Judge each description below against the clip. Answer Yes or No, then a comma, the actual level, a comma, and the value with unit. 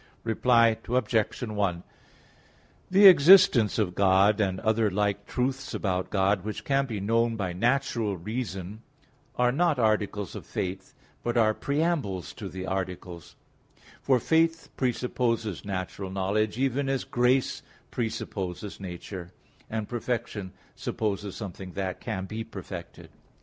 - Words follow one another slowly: Yes, slow, 125 wpm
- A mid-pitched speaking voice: No, low, 110 Hz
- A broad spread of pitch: No, average, 4.4 semitones